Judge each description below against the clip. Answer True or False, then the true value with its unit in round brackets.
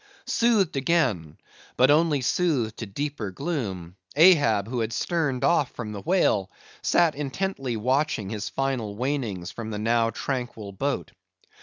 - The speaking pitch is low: True (125 Hz)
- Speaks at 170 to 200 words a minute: False (140 wpm)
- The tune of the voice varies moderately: False (5.9 semitones)